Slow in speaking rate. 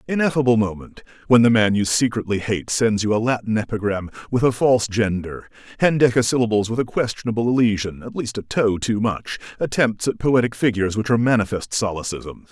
No: average, 165 wpm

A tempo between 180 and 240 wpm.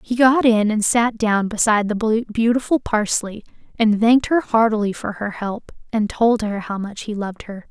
Yes: average, 195 wpm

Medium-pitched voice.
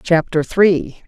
Yes: medium, 165 Hz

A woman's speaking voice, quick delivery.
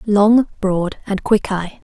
No: female; slow, 125 wpm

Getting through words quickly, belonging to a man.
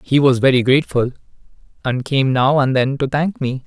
No: average, 195 wpm; male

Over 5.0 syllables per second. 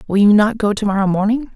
Yes: 6.5 syllables/s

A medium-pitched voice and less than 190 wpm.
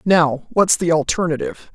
Yes: medium, 165 Hz; average, 140 wpm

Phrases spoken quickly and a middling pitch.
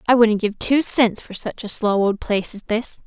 No: fast, 255 wpm; high, 220 Hz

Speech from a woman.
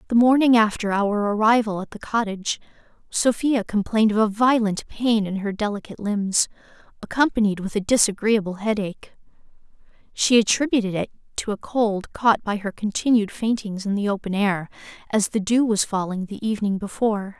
Yes: female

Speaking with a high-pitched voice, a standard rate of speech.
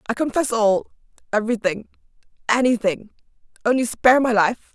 No: high, 230 Hz; slow, 90 wpm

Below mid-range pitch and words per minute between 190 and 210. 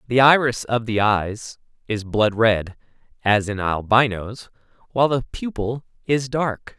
No: low, 115 Hz; average, 140 wpm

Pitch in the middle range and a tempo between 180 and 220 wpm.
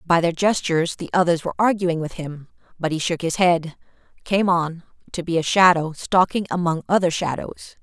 Yes: medium, 170 Hz; average, 185 wpm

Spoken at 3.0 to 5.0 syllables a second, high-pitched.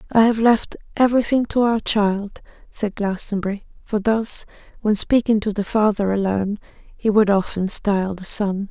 Yes: 4.8 syllables/s; high, 210 Hz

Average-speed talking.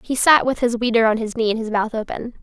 No: fast, 295 wpm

